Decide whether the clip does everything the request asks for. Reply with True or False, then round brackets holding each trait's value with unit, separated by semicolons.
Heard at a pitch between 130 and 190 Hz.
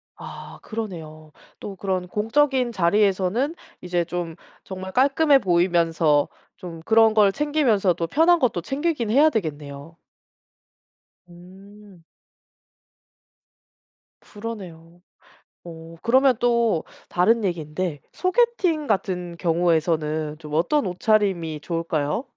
True (185 Hz)